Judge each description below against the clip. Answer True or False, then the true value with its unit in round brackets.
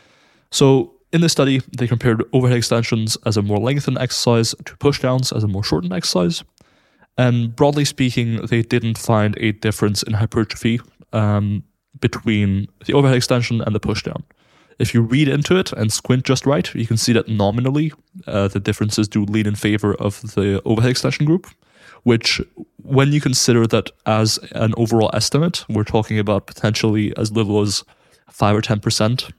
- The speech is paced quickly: False (170 wpm)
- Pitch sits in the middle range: False (115 Hz)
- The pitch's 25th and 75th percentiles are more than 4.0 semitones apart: False (3.4 semitones)